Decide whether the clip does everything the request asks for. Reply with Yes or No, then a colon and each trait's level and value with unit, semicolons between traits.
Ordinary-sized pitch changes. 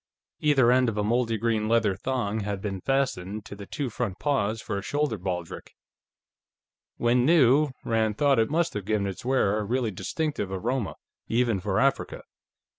Yes: average, 4.3 semitones